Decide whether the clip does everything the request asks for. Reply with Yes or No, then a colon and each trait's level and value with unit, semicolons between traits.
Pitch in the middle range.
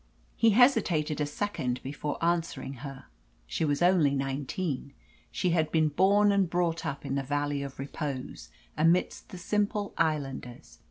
Yes: medium, 155 Hz